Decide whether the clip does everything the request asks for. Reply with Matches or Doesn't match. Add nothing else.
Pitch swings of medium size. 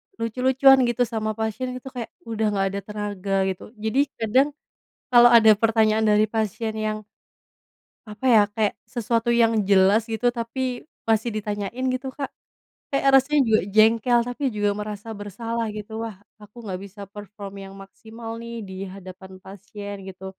Doesn't match